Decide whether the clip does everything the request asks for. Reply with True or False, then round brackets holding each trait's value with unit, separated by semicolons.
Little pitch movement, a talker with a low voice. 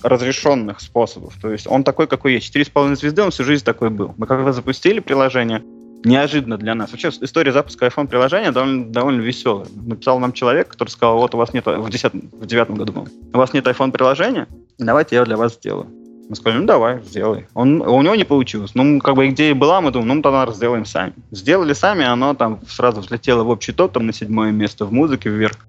False (3.1 semitones; 120 Hz)